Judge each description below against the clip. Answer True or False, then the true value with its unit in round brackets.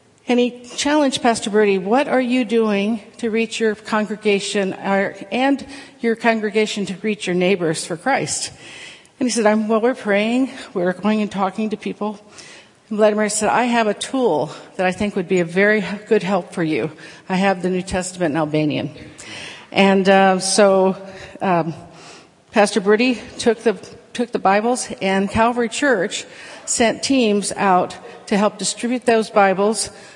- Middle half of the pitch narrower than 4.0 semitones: True (3.0 semitones)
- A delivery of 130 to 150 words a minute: False (160 wpm)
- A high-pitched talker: True (210 Hz)